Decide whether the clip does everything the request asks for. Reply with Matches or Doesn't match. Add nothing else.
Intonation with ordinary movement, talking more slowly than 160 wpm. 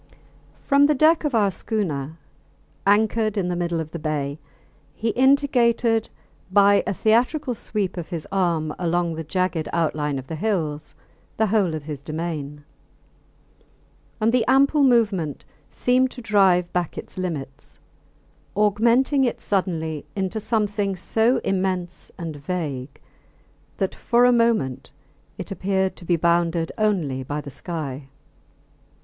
Doesn't match